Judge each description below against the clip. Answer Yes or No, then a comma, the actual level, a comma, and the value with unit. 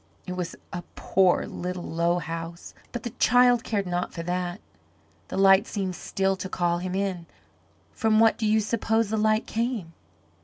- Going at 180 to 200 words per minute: No, average, 170 wpm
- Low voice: No, high, 190 Hz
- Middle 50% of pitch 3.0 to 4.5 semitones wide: Yes, average, 3.7 semitones